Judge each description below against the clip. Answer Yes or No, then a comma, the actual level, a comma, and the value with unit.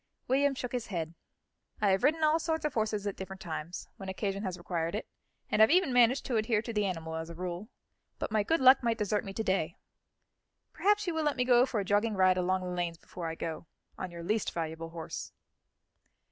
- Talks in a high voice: Yes, high, 205 Hz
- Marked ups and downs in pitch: Yes, wide, 5.9 semitones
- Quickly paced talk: Yes, fast, 225 wpm